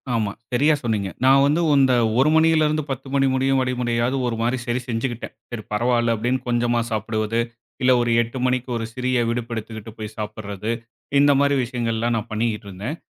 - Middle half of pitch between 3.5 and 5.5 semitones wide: No, narrow, 2.6 semitones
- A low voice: Yes, low, 120 Hz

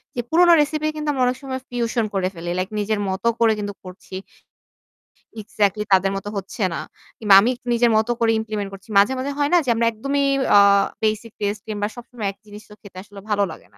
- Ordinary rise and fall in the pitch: Yes, average, 3.4 semitones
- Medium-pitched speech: No, high, 215 Hz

